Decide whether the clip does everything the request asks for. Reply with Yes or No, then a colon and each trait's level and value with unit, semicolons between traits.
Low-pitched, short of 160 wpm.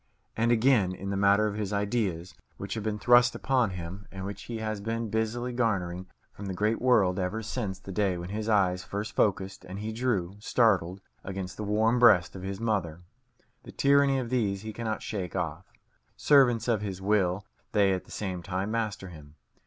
No: low, 105 Hz; average, 195 wpm